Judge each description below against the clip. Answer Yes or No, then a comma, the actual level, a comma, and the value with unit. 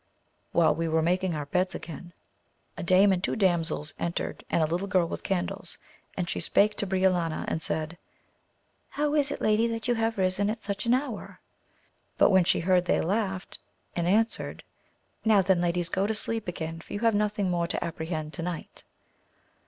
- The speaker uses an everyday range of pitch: Yes, average, 3.6 semitones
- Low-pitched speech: No, medium, 185 Hz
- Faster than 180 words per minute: Yes, average, 190 wpm